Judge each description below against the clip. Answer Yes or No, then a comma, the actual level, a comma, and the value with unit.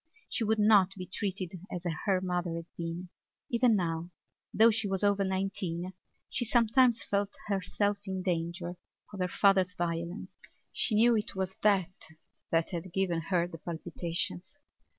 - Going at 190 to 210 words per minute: No, average, 150 wpm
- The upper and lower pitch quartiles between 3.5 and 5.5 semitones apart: No, average, 2.8 semitones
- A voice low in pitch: No, high, 190 Hz